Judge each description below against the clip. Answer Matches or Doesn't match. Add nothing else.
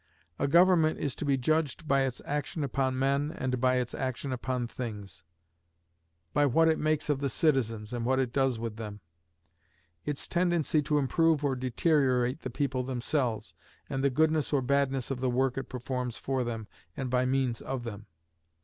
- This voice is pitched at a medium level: Doesn't match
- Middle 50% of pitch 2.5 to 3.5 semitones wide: Matches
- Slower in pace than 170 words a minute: Doesn't match